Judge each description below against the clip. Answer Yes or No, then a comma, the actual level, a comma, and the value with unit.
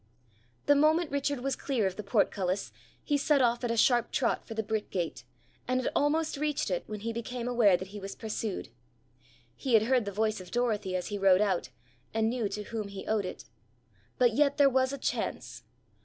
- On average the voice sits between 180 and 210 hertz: No, high, 225 Hz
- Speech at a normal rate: No, fast, 210 wpm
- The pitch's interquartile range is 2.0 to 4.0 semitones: No, average, 4.4 semitones